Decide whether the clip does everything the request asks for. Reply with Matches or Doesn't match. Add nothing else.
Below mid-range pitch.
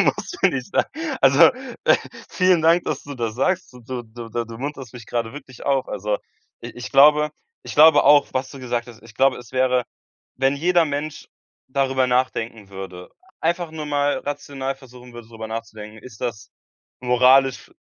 Matches